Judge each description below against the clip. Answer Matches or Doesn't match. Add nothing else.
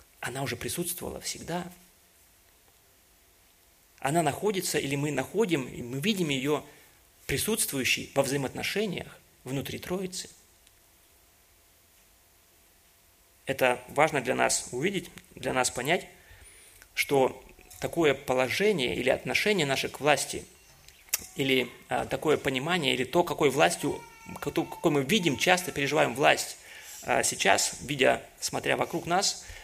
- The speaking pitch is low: Matches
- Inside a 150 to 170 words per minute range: Doesn't match